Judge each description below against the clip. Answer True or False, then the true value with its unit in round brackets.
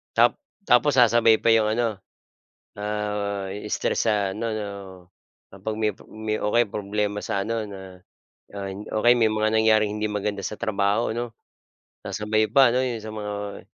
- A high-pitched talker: False (110 Hz)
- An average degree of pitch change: False (1.7 semitones)